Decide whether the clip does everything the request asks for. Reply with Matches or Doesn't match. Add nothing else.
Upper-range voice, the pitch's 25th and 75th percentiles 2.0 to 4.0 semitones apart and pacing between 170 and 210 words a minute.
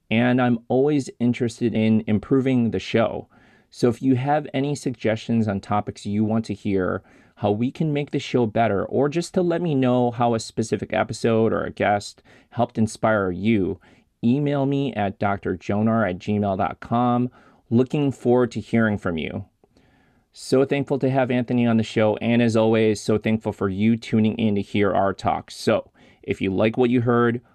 Doesn't match